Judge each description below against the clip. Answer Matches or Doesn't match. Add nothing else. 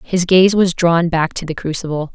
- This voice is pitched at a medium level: Matches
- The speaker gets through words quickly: Matches